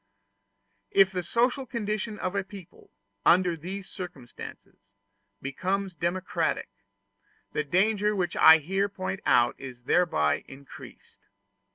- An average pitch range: Yes, average, 4.6 semitones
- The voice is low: No, medium, 185 Hz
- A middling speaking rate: No, slow, 110 wpm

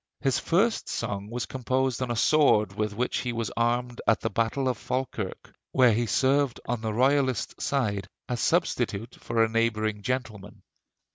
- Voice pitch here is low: Yes, low, 120 Hz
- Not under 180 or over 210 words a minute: No, average, 165 wpm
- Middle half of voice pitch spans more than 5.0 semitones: No, average, 3.2 semitones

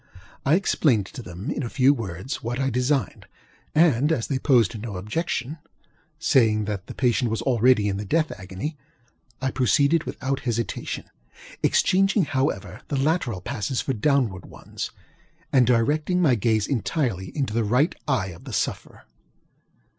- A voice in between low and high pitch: No, low, 125 Hz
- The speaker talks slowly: No, average, 150 wpm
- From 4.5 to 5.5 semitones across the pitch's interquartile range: Yes, average, 5.1 semitones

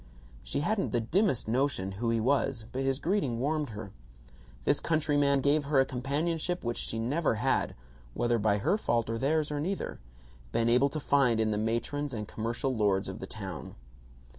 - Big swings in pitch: No, average, 4.4 semitones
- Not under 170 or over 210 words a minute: Yes, average, 185 wpm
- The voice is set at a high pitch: No, low, 130 Hz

